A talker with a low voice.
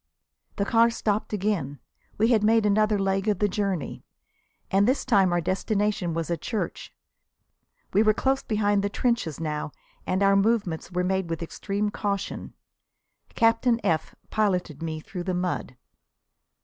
No: high, 200 Hz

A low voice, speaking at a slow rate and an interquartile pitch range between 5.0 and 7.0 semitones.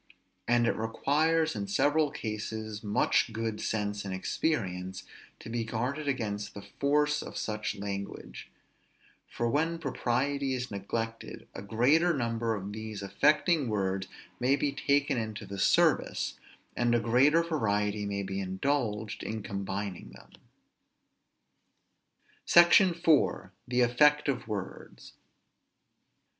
Yes: low, 115 Hz; slow, 125 wpm; wide, 5.6 semitones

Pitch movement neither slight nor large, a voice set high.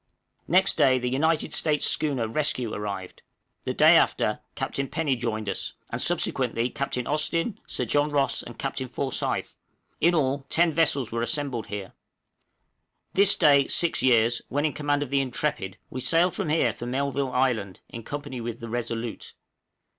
No: average, 4.0 semitones; low, 135 Hz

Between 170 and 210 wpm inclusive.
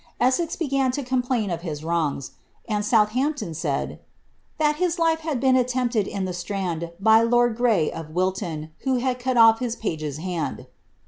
Yes: average, 180 wpm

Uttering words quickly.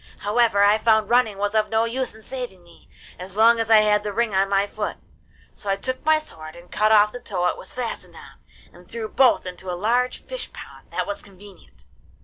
Yes: fast, 225 wpm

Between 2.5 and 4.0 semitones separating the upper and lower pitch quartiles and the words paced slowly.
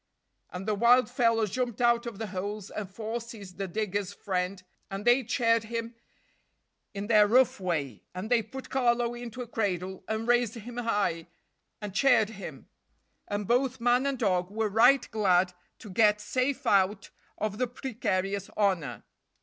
No: average, 3.4 semitones; average, 165 wpm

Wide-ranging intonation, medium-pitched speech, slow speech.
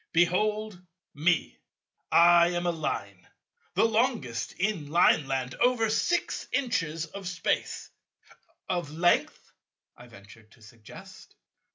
Yes: wide, 7.8 semitones; medium, 170 Hz; slow, 100 wpm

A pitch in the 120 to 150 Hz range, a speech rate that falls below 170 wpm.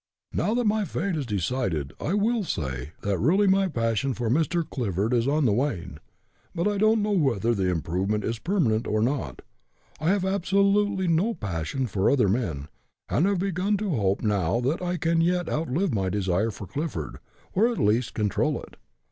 No: low, 135 Hz; average, 185 wpm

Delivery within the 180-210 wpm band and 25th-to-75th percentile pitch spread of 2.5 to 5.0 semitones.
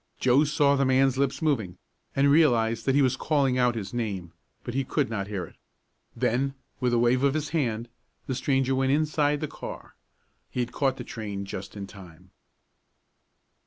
Yes: average, 185 wpm; average, 3.9 semitones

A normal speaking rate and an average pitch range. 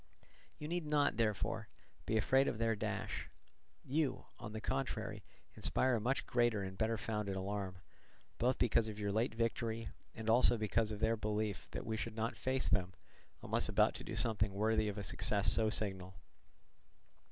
No: average, 170 wpm; narrow, 2.1 semitones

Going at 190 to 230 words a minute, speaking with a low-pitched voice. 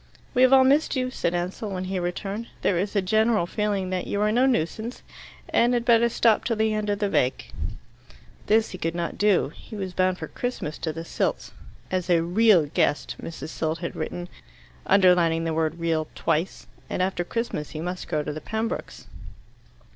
No: average, 195 wpm; medium, 185 Hz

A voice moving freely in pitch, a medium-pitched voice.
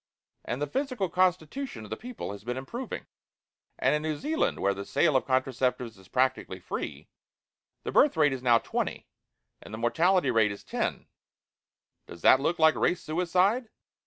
Yes: wide, 7.2 semitones; medium, 145 Hz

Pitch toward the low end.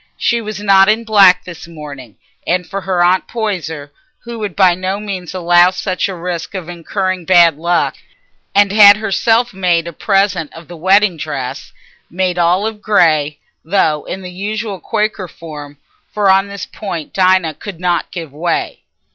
No: medium, 185 Hz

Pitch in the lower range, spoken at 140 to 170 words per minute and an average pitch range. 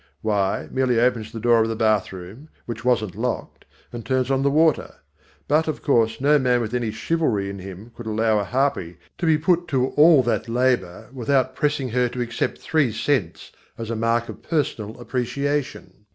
No: low, 120 Hz; average, 185 wpm; average, 4.0 semitones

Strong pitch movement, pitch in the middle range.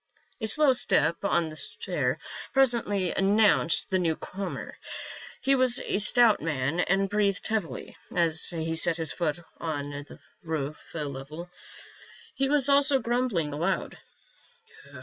Yes: wide, 5.8 semitones; medium, 180 Hz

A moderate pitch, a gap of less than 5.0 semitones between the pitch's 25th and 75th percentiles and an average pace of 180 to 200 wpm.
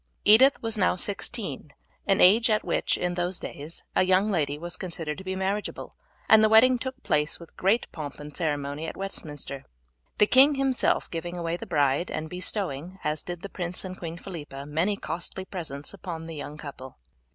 Yes: medium, 175 Hz; average, 4.6 semitones; average, 185 wpm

